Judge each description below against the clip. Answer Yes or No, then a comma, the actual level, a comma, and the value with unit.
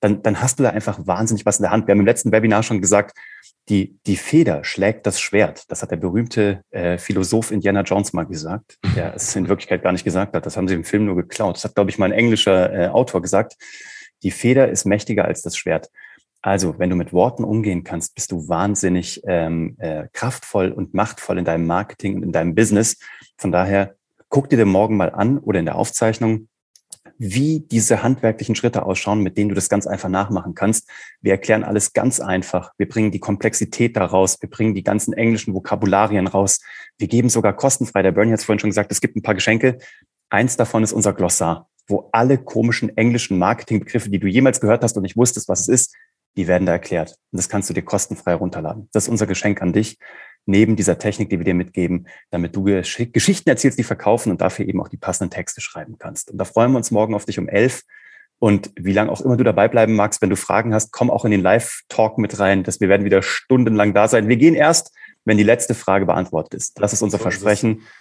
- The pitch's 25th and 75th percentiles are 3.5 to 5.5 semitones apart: No, average, 2.8 semitones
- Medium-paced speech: No, fast, 230 wpm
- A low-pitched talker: Yes, low, 105 Hz